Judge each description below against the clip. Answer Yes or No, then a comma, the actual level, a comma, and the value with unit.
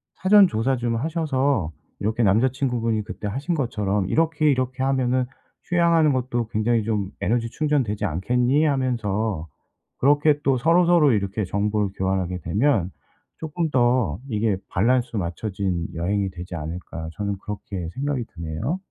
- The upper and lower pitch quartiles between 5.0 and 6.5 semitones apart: Yes, wide, 5.6 semitones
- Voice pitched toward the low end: Yes, low, 115 Hz